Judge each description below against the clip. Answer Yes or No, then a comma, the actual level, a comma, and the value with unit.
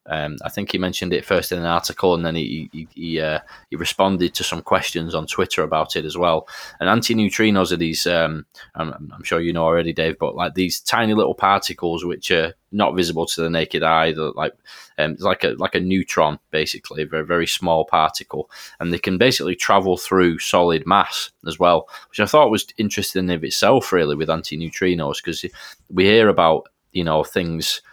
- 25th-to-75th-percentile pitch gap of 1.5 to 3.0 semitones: Yes, narrow, 2.5 semitones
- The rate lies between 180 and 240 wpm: Yes, average, 200 wpm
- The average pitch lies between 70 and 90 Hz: Yes, very low, 85 Hz